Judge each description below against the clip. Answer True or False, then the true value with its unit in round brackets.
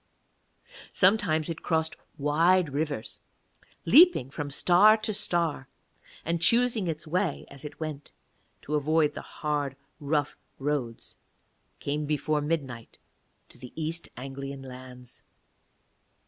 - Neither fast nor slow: False (115 wpm)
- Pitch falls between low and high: True (150 Hz)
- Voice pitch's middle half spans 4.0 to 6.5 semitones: False (3.3 semitones)